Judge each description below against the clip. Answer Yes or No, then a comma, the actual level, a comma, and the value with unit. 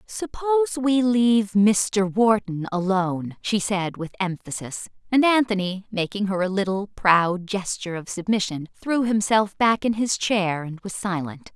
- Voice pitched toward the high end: Yes, high, 200 Hz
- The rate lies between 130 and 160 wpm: Yes, average, 150 wpm